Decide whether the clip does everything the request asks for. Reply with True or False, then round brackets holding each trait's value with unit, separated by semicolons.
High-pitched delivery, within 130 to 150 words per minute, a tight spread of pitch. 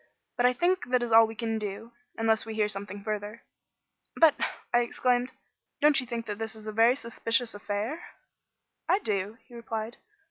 False (225 Hz; 180 wpm; 2.3 semitones)